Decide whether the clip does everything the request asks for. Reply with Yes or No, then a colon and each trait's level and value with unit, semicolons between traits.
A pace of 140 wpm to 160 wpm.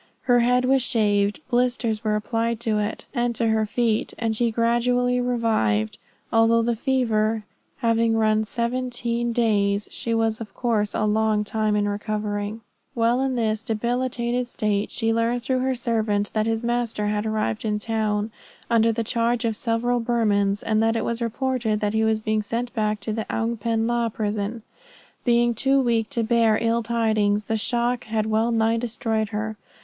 No: average, 175 wpm